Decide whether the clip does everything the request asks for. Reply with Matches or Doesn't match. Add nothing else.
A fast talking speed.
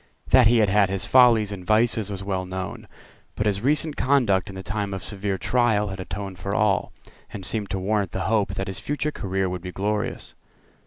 Matches